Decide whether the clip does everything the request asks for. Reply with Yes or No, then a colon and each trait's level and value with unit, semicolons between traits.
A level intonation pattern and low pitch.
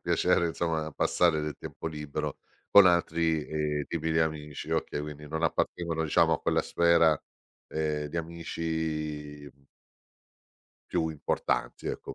Yes: narrow, 1.6 semitones; very low, 80 Hz